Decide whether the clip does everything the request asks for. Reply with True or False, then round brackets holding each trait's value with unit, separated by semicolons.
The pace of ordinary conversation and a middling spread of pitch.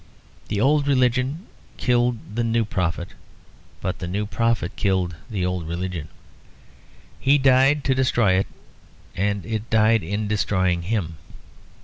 False (130 wpm; 5.0 semitones)